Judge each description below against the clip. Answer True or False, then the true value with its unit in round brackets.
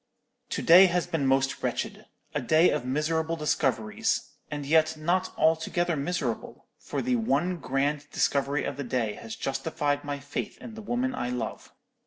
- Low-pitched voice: False (150 Hz)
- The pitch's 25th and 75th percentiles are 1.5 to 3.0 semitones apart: False (4.1 semitones)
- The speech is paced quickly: False (160 wpm)